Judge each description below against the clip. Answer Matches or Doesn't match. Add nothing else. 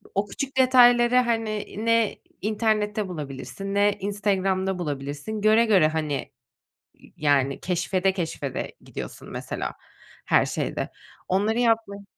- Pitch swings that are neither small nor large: Matches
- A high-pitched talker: Matches